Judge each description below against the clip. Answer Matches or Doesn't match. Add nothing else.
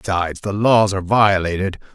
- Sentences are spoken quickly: Doesn't match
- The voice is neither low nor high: Doesn't match